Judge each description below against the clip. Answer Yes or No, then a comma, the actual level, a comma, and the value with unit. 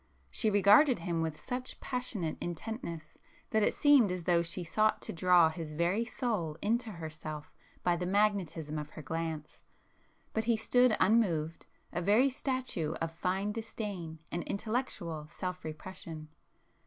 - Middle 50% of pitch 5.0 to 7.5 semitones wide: Yes, average, 5.3 semitones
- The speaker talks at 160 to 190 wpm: No, average, 140 wpm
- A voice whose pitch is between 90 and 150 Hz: No, medium, 180 Hz